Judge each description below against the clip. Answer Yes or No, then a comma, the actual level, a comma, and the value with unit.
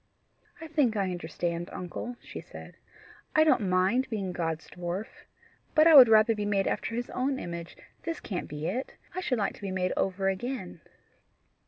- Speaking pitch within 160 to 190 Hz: No, high, 200 Hz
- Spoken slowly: No, average, 180 wpm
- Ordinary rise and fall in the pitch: No, wide, 5.8 semitones